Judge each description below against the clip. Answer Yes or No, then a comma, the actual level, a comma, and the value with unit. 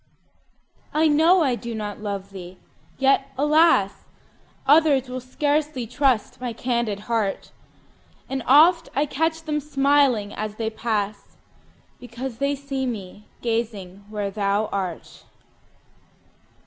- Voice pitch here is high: Yes, high, 245 Hz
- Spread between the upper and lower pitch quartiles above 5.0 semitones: Yes, wide, 5.4 semitones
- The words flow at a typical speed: No, slow, 120 wpm